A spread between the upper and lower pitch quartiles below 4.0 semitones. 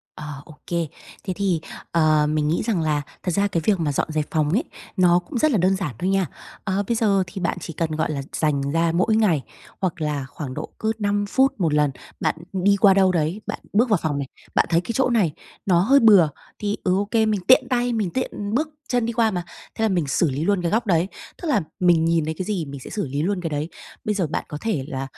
No: average, 4.9 semitones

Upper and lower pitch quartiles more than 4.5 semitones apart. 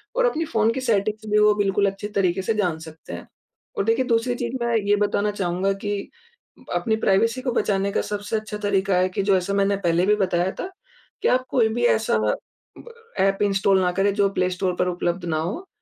No: average, 3.2 semitones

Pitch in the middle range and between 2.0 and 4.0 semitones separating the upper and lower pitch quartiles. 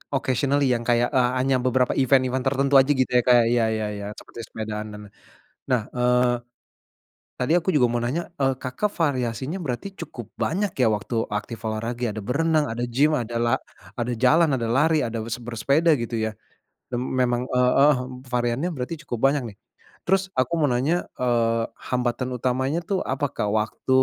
No: low, 125 Hz; average, 2.8 semitones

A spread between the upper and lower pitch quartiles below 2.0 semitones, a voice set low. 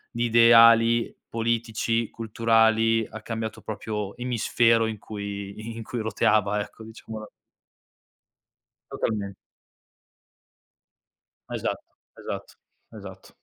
Yes: narrow, 1.3 semitones; low, 115 Hz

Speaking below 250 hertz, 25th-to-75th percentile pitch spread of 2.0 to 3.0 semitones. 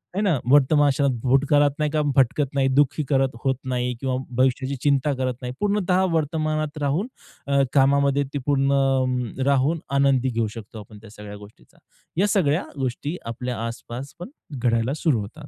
Yes: medium, 140 Hz; narrow, 2.6 semitones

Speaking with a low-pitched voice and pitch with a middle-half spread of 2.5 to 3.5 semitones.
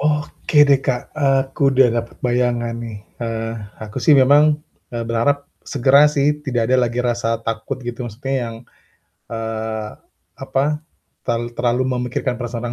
Yes: low, 125 Hz; average, 3.0 semitones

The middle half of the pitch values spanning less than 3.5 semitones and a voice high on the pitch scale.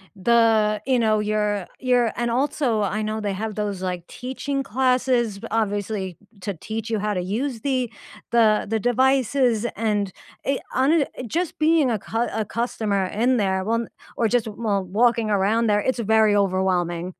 Yes: average, 3.1 semitones; high, 220 Hz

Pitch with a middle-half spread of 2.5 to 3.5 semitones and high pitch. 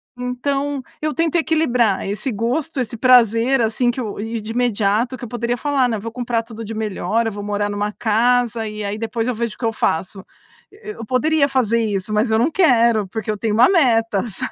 Yes: average, 2.8 semitones; high, 230 Hz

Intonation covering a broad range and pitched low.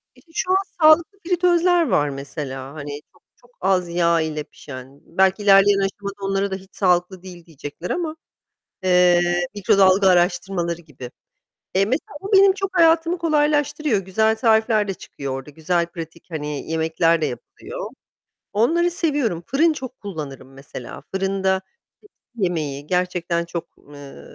No: wide, 7.0 semitones; medium, 185 Hz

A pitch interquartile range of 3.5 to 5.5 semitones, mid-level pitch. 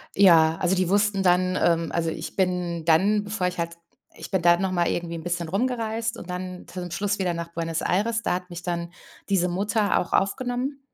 No: average, 2.9 semitones; medium, 180 Hz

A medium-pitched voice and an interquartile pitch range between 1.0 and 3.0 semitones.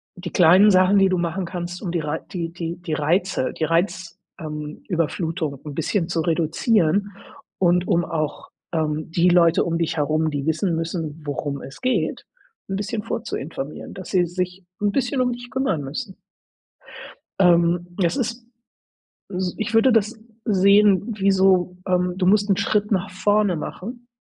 No: medium, 180 Hz; average, 3.5 semitones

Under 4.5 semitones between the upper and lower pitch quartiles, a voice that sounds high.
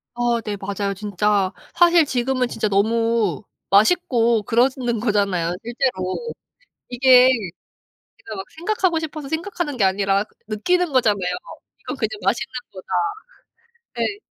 No: average, 5.2 semitones; high, 230 Hz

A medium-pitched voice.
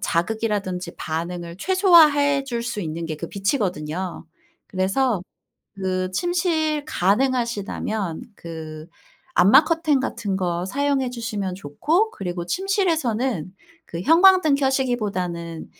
No: high, 210 Hz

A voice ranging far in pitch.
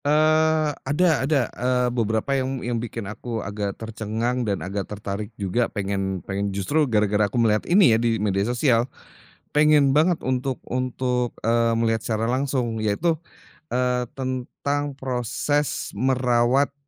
No: average, 3.9 semitones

